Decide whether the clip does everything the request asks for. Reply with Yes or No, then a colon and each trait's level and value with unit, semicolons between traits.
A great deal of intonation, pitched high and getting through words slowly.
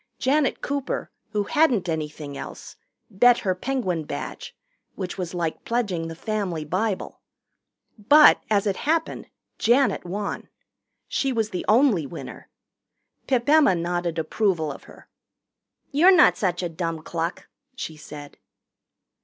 Yes: wide, 6.7 semitones; high, 195 Hz; slow, 130 wpm